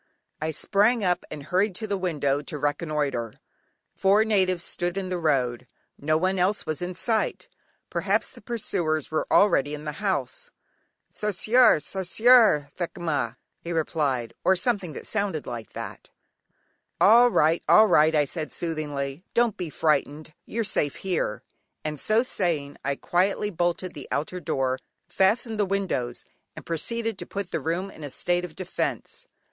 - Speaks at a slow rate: No, average, 155 wpm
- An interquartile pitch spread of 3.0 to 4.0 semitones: No, average, 5.0 semitones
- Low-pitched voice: No, medium, 175 Hz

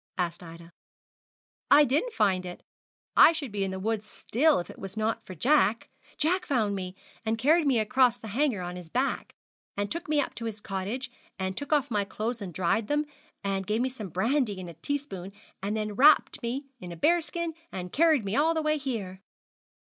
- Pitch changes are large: Yes, wide, 7.0 semitones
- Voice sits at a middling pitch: No, high, 220 Hz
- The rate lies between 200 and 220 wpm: Yes, fast, 205 wpm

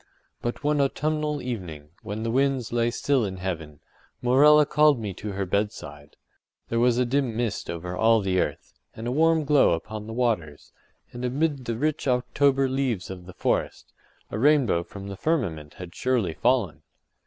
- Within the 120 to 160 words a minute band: No, average, 175 wpm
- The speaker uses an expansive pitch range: Yes, wide, 6.4 semitones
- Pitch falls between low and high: No, low, 120 Hz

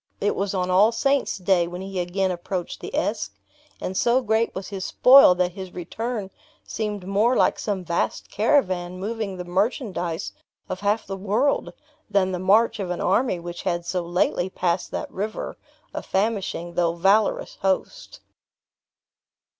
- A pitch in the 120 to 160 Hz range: No, high, 190 Hz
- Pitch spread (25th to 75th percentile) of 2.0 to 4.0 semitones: Yes, average, 3.1 semitones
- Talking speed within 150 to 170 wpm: Yes, average, 160 wpm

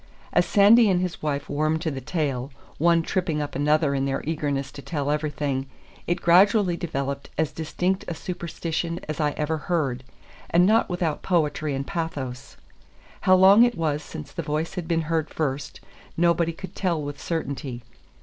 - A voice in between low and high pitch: Yes, medium, 155 Hz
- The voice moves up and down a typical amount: Yes, average, 3.2 semitones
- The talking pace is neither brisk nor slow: Yes, average, 170 wpm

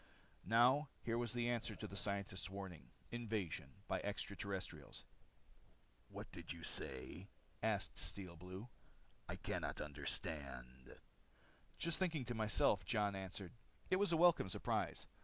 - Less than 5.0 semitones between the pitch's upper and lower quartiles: No, average, 5.3 semitones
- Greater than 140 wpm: No, slow, 135 wpm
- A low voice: Yes, low, 100 Hz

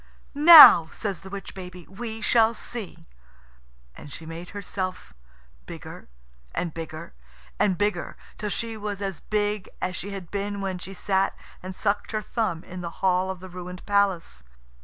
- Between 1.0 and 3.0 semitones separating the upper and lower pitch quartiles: Yes, narrow, 2.4 semitones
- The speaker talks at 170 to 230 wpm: No, average, 160 wpm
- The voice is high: Yes, high, 195 Hz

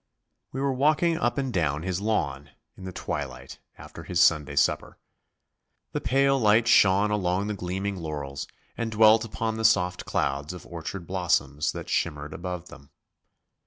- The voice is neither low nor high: No, very low, 95 Hz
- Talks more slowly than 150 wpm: No, average, 160 wpm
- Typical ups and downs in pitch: No, wide, 5.7 semitones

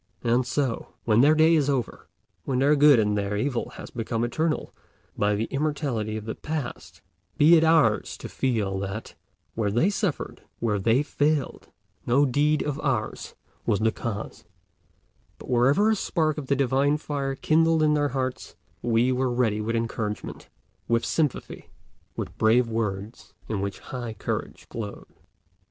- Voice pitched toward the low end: Yes, low, 125 Hz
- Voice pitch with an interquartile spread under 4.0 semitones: No, average, 4.8 semitones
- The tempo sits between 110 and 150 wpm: No, average, 160 wpm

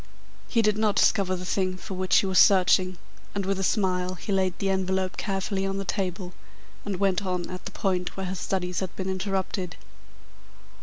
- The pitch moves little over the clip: Yes, narrow, 1.1 semitones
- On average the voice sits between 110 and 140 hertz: No, high, 190 Hz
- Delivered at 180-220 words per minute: Yes, average, 195 wpm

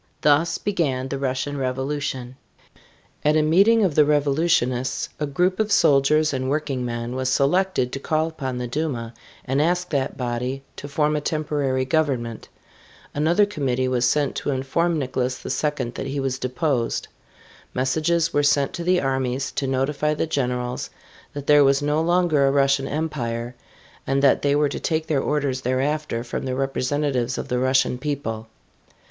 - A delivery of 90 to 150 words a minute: No, average, 165 wpm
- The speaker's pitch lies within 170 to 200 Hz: No, medium, 140 Hz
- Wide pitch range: No, average, 2.8 semitones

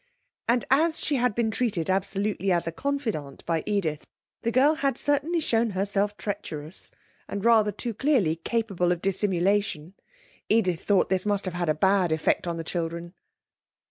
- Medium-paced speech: Yes, average, 160 wpm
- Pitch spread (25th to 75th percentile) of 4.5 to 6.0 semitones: Yes, average, 5.1 semitones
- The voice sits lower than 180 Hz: No, high, 200 Hz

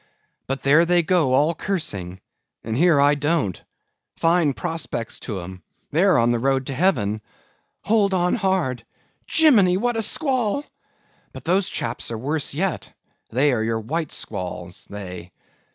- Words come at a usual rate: Yes, average, 150 wpm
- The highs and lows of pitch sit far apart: Yes, wide, 8.0 semitones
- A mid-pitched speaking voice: Yes, medium, 145 Hz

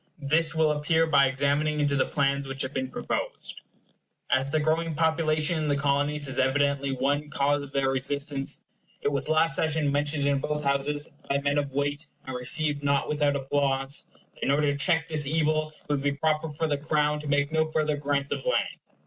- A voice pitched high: No, medium, 145 Hz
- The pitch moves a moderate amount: No, narrow, 1.7 semitones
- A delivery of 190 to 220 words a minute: Yes, average, 200 wpm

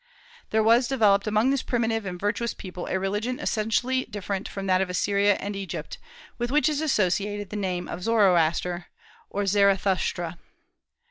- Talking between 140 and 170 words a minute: Yes, average, 155 wpm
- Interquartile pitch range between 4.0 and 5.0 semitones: No, average, 3.2 semitones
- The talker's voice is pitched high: Yes, high, 205 Hz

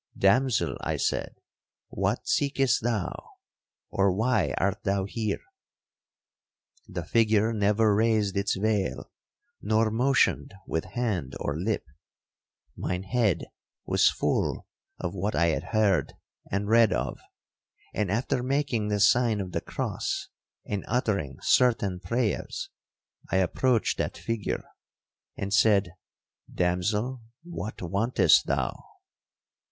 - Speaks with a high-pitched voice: No, low, 105 Hz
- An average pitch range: Yes, average, 3.2 semitones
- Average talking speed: No, slow, 115 wpm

